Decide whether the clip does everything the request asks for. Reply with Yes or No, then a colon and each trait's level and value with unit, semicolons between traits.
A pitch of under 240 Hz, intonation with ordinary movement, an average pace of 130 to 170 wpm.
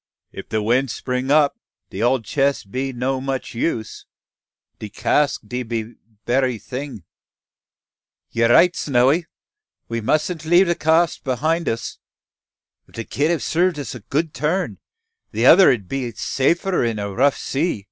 Yes: low, 135 Hz; average, 4.9 semitones; average, 155 wpm